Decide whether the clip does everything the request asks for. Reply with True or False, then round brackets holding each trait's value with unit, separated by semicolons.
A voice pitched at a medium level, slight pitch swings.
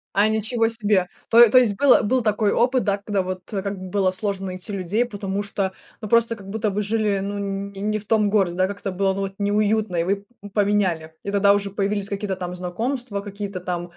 False (200 Hz; 1.8 semitones)